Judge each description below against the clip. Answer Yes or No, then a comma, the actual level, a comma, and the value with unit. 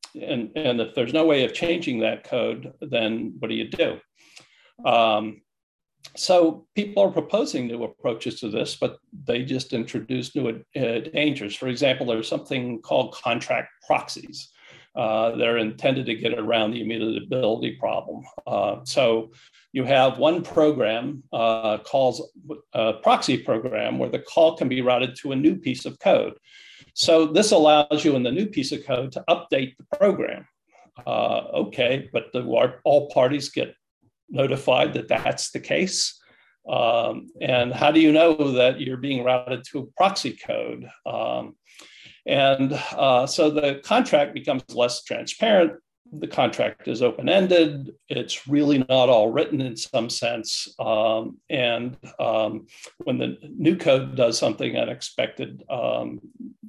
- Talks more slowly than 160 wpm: Yes, average, 150 wpm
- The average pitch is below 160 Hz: Yes, low, 135 Hz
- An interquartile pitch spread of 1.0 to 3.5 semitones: No, average, 4.8 semitones